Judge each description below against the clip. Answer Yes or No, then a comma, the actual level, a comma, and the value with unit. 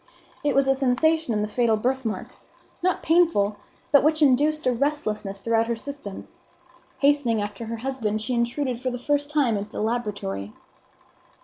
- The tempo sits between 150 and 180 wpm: Yes, average, 165 wpm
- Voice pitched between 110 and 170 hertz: No, high, 245 Hz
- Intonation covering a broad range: No, average, 4.9 semitones